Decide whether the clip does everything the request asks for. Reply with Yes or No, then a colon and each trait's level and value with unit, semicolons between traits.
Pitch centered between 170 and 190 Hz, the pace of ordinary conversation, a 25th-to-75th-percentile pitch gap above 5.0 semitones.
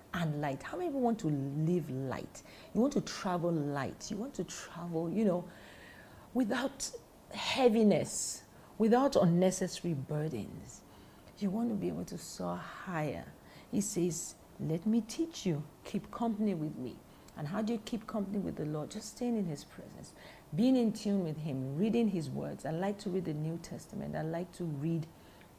Yes: medium, 185 Hz; average, 175 wpm; wide, 5.6 semitones